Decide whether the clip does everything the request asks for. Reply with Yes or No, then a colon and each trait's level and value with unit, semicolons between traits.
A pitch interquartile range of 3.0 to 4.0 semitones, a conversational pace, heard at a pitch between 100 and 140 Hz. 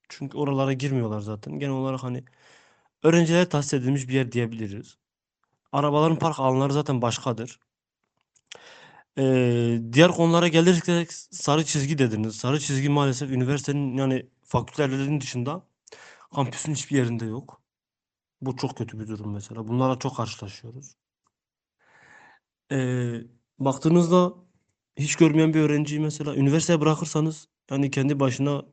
Yes: average, 3.6 semitones; average, 120 wpm; low, 135 Hz